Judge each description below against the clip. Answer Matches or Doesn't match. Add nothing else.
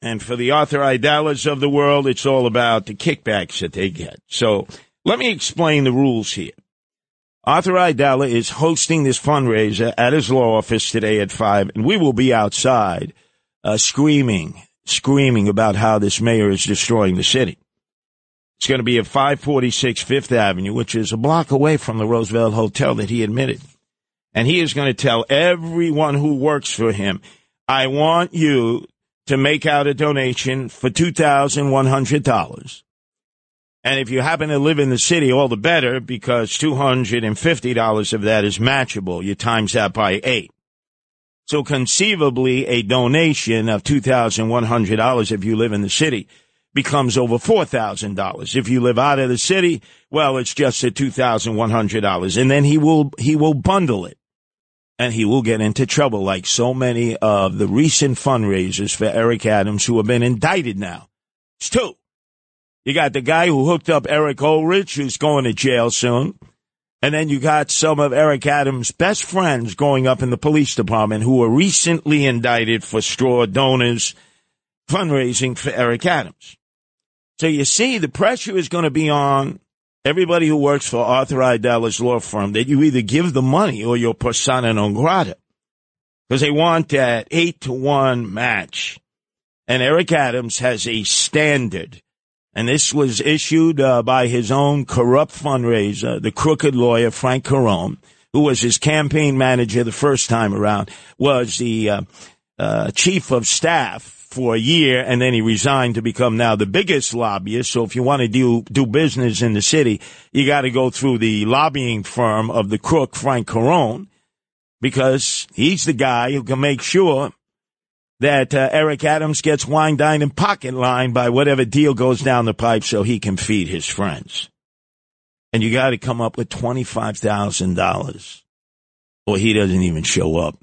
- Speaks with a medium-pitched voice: Doesn't match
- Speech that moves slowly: Doesn't match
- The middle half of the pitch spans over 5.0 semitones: Doesn't match